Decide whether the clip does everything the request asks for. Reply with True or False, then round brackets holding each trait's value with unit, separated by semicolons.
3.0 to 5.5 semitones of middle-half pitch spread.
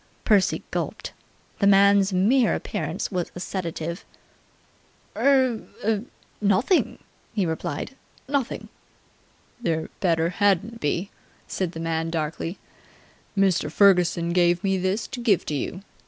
True (3.4 semitones)